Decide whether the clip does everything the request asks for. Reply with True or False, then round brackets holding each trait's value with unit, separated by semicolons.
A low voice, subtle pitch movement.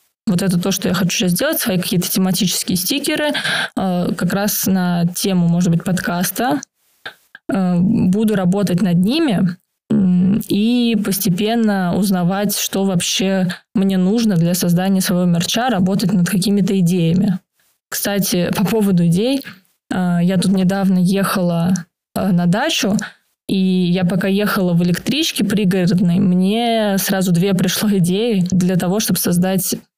False (190 Hz; 2.3 semitones)